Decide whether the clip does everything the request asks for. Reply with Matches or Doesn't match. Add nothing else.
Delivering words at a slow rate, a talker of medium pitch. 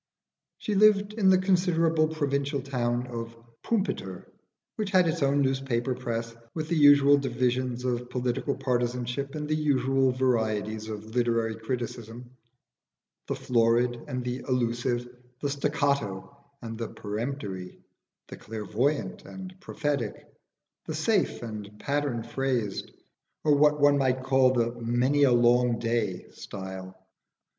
Doesn't match